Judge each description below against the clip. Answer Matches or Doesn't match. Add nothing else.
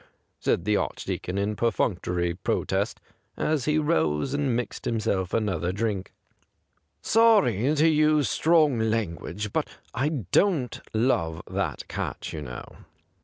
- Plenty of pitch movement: Matches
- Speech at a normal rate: Doesn't match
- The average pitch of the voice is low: Matches